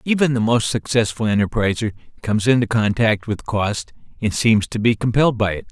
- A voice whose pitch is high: No, low, 115 Hz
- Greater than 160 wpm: Yes, average, 180 wpm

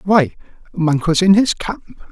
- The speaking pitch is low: No, medium, 175 Hz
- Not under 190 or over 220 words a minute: No, average, 170 wpm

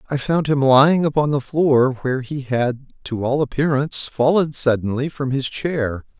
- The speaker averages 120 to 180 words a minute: Yes, average, 175 wpm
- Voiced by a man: Yes, male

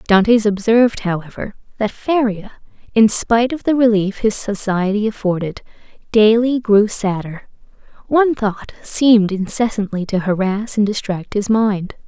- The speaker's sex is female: Yes, female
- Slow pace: Yes, slow, 130 wpm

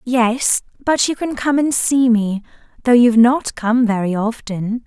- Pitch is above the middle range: Yes, high, 240 Hz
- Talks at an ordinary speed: Yes, average, 175 wpm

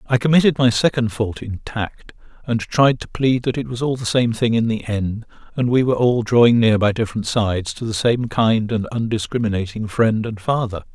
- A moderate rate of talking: No, fast, 215 wpm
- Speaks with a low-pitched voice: Yes, low, 115 Hz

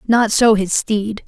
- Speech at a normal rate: Yes, average, 190 wpm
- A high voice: Yes, high, 215 Hz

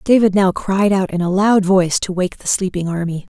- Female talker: Yes, female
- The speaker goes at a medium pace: No, fast, 235 wpm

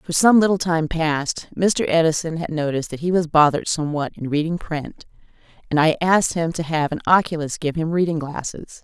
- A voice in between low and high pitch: Yes, medium, 160 Hz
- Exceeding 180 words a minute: Yes, average, 195 wpm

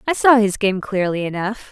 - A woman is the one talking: Yes, female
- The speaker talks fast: Yes, fast, 210 wpm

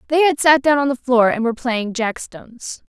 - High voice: Yes, very high, 255 Hz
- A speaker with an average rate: No, fast, 245 wpm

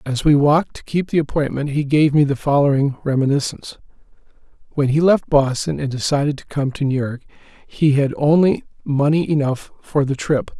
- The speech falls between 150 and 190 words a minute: Yes, average, 180 wpm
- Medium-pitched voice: Yes, medium, 145 Hz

